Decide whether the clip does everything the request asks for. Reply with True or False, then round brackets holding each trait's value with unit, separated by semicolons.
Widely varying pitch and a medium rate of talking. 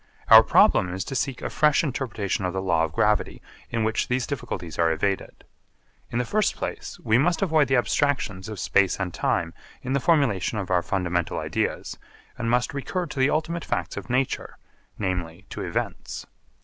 True (6.9 semitones; 185 wpm)